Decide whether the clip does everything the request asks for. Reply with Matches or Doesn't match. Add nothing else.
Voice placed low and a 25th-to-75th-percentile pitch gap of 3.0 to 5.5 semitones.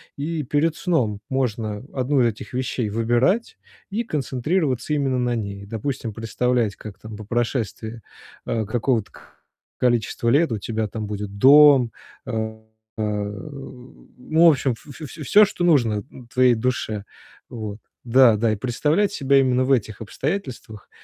Matches